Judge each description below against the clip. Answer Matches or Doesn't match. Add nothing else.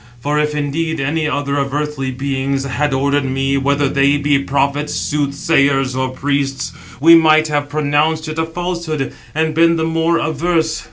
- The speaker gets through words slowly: Doesn't match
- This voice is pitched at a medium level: Matches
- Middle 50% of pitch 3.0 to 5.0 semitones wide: Doesn't match